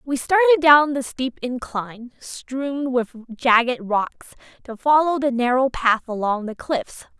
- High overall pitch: Yes, very high, 255 Hz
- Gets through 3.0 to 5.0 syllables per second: Yes, 3.8 syllables/s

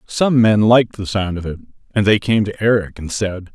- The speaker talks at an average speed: No, fast, 235 wpm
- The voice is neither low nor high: No, low, 105 Hz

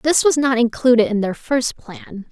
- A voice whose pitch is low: No, high, 245 Hz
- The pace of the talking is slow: No, fast, 205 wpm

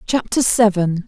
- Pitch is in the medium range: No, high, 205 Hz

